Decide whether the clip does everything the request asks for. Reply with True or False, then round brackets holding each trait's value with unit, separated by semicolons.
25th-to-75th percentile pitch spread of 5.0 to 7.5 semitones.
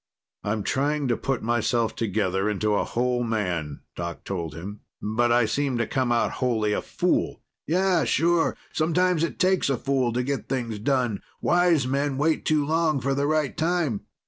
True (5.6 semitones)